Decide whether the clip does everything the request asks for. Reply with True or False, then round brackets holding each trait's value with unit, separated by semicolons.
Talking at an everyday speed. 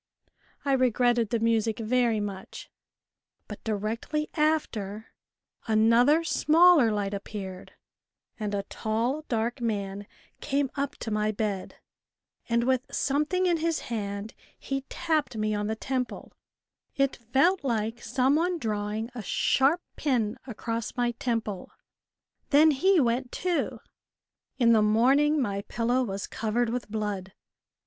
False (130 wpm)